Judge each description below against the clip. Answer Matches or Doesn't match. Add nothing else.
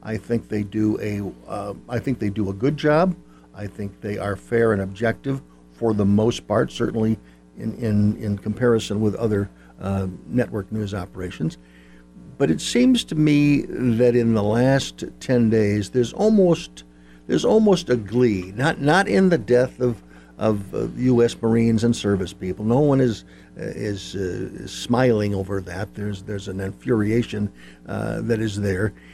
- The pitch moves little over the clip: Doesn't match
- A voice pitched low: Matches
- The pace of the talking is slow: Doesn't match